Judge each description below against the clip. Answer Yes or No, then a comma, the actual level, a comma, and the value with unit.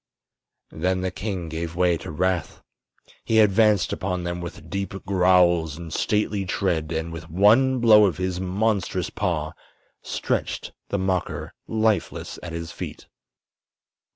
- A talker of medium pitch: No, very low, 90 Hz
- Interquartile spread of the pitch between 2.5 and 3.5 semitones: Yes, average, 3.0 semitones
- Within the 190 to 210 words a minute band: No, slow, 135 wpm